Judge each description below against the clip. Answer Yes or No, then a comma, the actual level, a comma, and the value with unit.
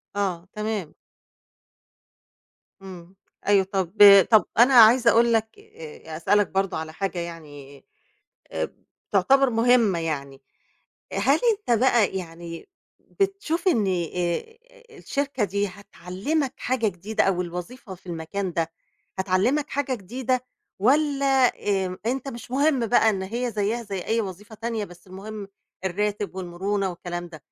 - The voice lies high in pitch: Yes, high, 200 Hz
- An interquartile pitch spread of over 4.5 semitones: Yes, average, 5.2 semitones